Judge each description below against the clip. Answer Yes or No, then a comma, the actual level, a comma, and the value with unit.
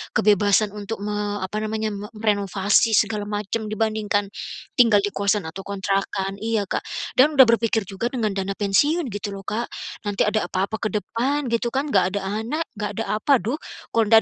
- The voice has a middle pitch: No, high, 210 Hz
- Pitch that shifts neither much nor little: No, narrow, 2.1 semitones